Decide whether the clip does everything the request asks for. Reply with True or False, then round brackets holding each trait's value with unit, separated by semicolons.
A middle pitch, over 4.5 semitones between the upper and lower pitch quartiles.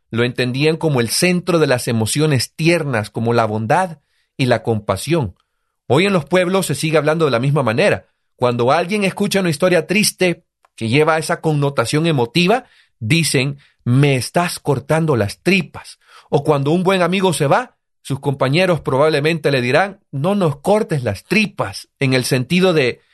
True (155 Hz; 5.4 semitones)